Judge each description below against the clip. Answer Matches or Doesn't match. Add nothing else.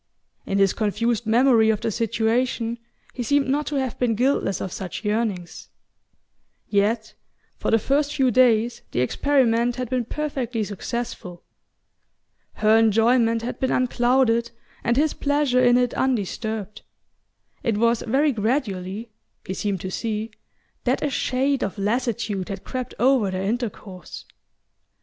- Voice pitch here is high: Matches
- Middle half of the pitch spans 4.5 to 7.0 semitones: Doesn't match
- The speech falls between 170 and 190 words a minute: Doesn't match